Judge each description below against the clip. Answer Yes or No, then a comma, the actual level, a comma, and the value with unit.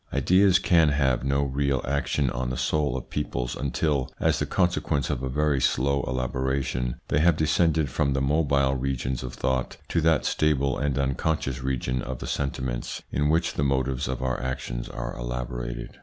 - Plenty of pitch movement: No, narrow, 2.5 semitones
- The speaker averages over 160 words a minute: Yes, average, 175 wpm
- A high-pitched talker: No, very low, 65 Hz